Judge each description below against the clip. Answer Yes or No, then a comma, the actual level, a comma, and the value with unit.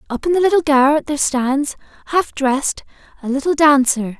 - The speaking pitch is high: Yes, very high, 285 Hz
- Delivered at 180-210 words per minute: No, average, 170 wpm